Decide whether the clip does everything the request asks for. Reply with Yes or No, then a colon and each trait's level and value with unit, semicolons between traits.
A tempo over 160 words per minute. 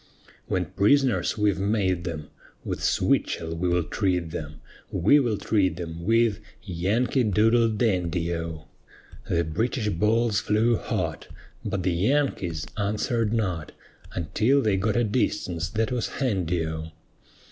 No: slow, 135 wpm